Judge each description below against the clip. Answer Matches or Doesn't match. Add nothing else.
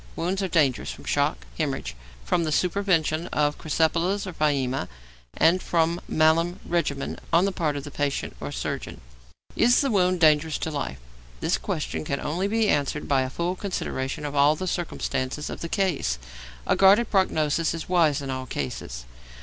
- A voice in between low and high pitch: Matches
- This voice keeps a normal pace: Matches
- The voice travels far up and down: Doesn't match